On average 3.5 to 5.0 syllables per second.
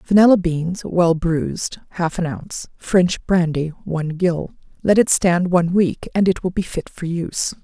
Yes: 4.5 syllables/s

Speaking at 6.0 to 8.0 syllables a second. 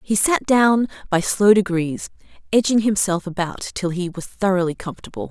No: 5.1 syllables/s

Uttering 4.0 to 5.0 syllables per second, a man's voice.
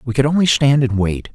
No: 5.7 syllables/s; male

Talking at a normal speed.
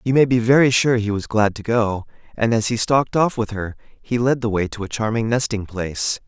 No: fast, 250 wpm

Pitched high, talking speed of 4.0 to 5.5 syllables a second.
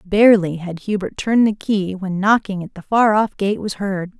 Yes: high, 200 Hz; 5.0 syllables/s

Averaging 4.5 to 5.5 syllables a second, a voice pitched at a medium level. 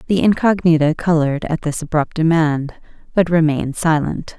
Yes: 5.2 syllables/s; medium, 160 Hz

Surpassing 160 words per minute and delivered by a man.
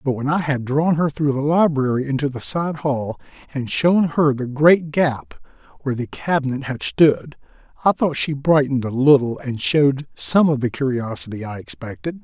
Yes: average, 185 wpm; male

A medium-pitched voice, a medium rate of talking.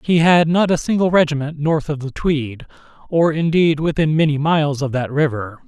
Yes: medium, 150 Hz; average, 190 wpm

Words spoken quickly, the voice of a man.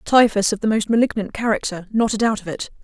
No: fast, 210 wpm; female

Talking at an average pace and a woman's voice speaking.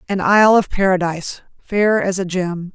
Yes: average, 175 wpm; female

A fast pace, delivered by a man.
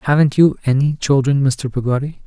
No: average, 160 wpm; male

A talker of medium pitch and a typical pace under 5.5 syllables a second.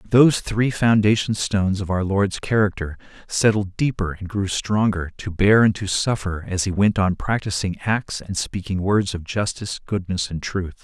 No: low, 100 Hz; 4.8 syllables/s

